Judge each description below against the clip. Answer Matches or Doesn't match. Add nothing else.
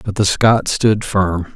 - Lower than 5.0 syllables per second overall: Matches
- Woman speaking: Doesn't match